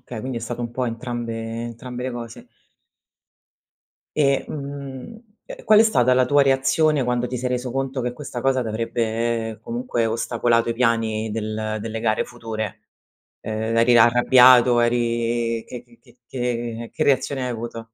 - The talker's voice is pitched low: Yes, low, 120 Hz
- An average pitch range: No, narrow, 2.0 semitones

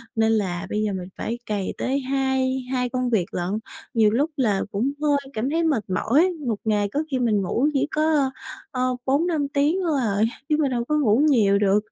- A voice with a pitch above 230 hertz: Yes, very high, 250 Hz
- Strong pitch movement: No, average, 5.0 semitones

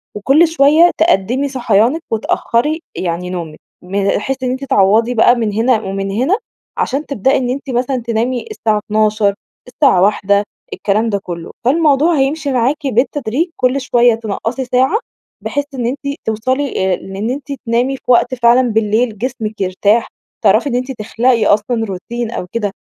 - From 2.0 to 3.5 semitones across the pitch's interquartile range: No, average, 4.1 semitones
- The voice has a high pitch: Yes, high, 240 Hz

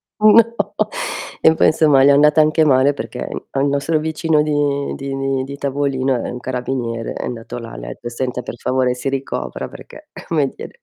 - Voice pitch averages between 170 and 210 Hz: No, medium, 140 Hz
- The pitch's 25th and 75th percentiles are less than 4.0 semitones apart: Yes, average, 2.8 semitones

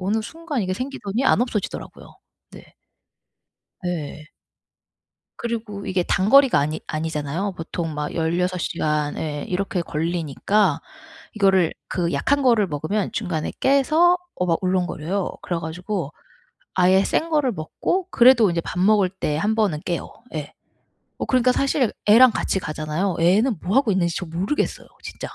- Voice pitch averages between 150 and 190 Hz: Yes, medium, 185 Hz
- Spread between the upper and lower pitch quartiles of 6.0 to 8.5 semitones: No, wide, 5.4 semitones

